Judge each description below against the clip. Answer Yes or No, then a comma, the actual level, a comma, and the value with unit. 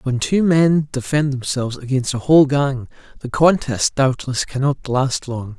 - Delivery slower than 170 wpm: Yes, average, 160 wpm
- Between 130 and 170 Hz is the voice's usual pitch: Yes, low, 135 Hz